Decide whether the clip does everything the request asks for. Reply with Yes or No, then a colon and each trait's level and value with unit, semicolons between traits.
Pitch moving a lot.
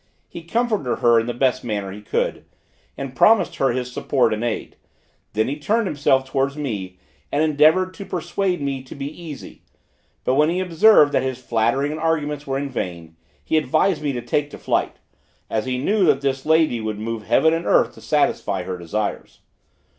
No: average, 4.9 semitones